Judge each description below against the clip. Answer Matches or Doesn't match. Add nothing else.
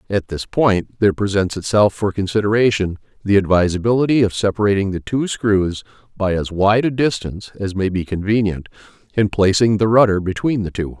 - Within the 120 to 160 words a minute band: Doesn't match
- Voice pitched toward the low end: Matches